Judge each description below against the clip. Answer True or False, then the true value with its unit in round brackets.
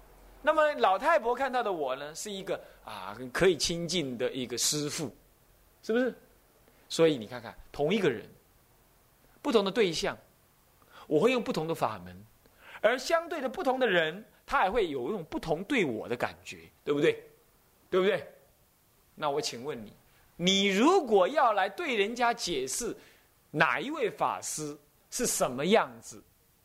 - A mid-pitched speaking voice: True (175 Hz)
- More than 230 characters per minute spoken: False (225 characters per minute)